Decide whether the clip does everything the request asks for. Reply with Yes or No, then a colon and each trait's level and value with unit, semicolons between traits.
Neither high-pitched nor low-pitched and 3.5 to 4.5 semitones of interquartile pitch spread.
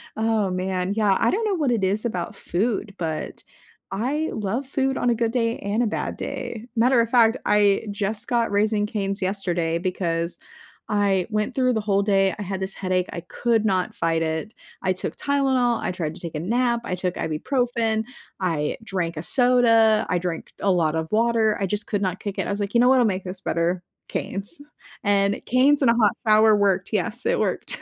No: high, 205 Hz; average, 4.0 semitones